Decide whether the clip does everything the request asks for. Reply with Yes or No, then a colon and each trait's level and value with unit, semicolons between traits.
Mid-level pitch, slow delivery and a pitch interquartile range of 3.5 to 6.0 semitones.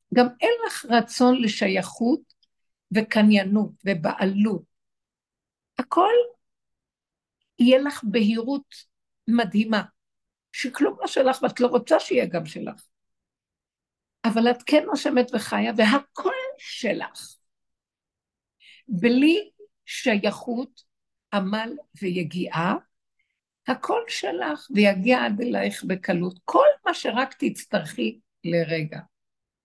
No: high, 235 Hz; slow, 85 wpm; wide, 5.5 semitones